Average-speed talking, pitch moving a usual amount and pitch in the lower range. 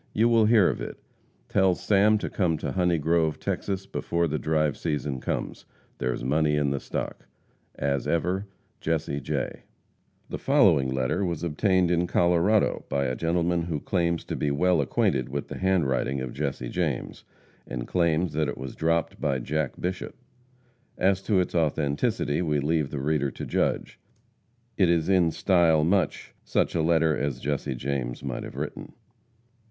Yes: average, 165 wpm; average, 3.9 semitones; very low, 80 Hz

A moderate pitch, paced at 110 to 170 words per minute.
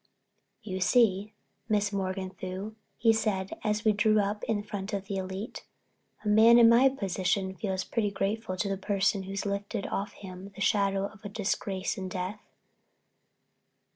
No: high, 200 Hz; average, 155 wpm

